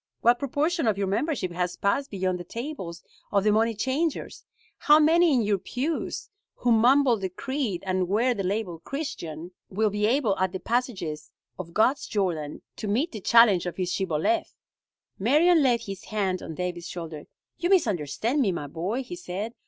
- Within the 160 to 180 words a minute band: Yes, average, 175 wpm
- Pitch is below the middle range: No, high, 210 Hz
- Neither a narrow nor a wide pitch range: No, wide, 6.4 semitones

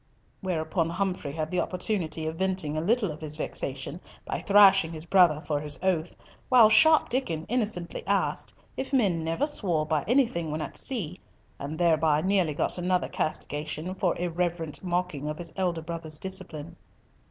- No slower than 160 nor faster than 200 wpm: Yes, average, 165 wpm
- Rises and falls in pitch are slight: No, average, 3.4 semitones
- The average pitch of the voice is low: No, medium, 170 Hz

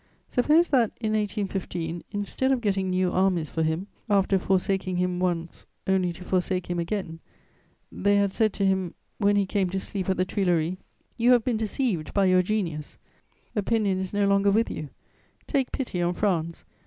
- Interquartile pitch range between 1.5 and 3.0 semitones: Yes, narrow, 2.6 semitones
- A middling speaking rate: Yes, average, 180 wpm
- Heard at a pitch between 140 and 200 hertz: Yes, high, 190 Hz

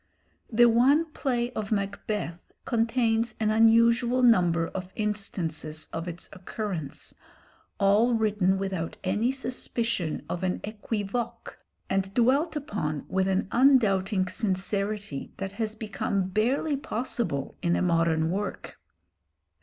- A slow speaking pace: Yes, slow, 115 wpm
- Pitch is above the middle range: Yes, high, 210 Hz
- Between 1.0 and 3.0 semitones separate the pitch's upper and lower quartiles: No, average, 3.9 semitones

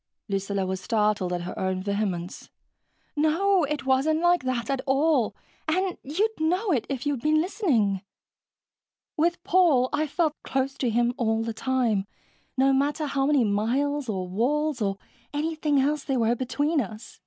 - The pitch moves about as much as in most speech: No, wide, 5.8 semitones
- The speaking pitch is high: Yes, very high, 270 Hz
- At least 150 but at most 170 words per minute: Yes, average, 160 wpm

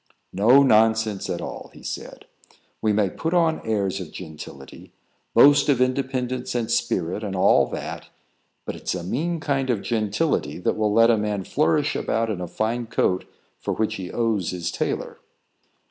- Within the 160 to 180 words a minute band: Yes, average, 170 wpm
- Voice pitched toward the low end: Yes, low, 110 Hz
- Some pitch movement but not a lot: Yes, average, 4.7 semitones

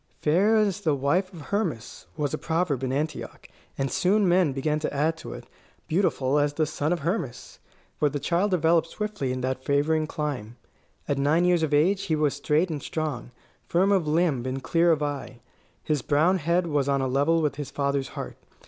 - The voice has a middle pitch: Yes, medium, 150 Hz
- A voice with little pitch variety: No, average, 3.6 semitones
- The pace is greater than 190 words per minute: Yes, average, 200 wpm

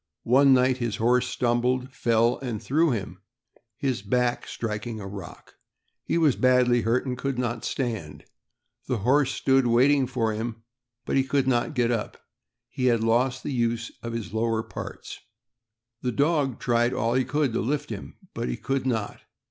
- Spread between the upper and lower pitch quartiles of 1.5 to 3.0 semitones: Yes, narrow, 2.5 semitones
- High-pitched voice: No, low, 125 Hz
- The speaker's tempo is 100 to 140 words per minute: No, average, 170 wpm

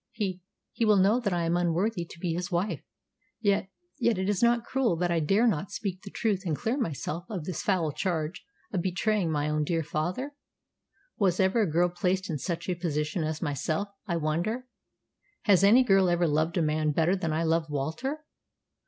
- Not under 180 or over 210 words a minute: Yes, average, 200 wpm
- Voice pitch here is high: No, medium, 180 Hz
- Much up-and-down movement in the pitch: No, average, 3.8 semitones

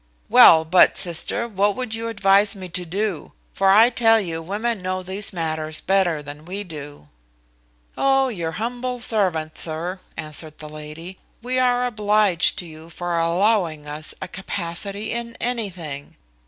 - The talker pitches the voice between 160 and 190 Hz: Yes, medium, 185 Hz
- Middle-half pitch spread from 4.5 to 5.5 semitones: Yes, average, 5.0 semitones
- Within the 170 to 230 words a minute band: No, average, 155 wpm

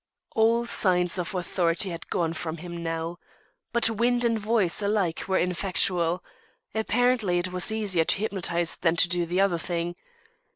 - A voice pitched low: No, medium, 180 Hz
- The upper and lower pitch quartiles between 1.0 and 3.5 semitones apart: No, average, 3.9 semitones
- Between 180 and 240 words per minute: No, average, 160 wpm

